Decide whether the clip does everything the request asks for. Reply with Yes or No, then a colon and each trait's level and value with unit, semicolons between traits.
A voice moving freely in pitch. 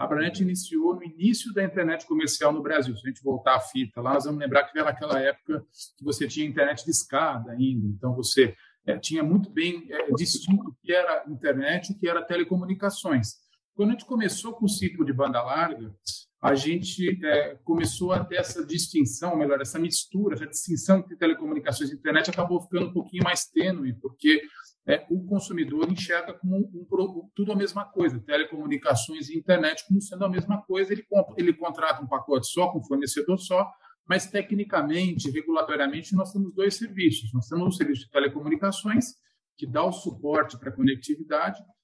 No: average, 4.7 semitones